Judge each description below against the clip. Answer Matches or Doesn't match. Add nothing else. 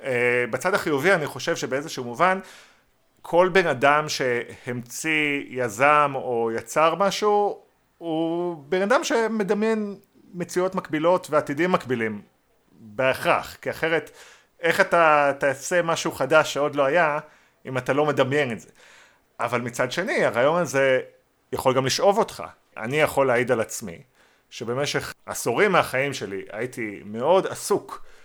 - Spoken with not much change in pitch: Doesn't match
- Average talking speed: Matches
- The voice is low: Doesn't match